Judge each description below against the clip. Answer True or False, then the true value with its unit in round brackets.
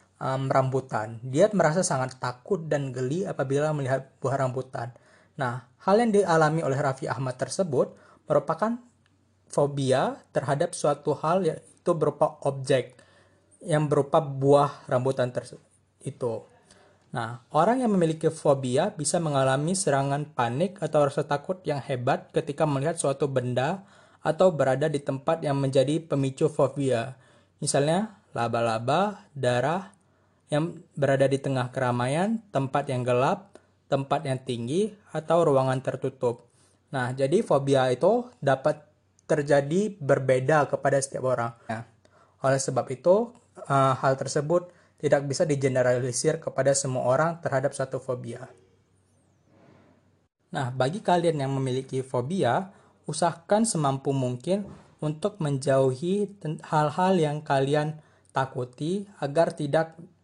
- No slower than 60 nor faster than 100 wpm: False (120 wpm)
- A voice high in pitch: False (140 Hz)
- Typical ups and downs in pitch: True (3.7 semitones)